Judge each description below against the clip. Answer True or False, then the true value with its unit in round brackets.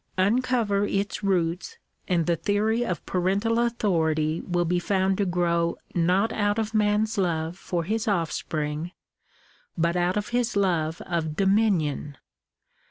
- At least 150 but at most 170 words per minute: False (140 wpm)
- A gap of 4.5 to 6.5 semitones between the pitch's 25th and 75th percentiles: False (3.7 semitones)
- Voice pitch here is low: False (185 Hz)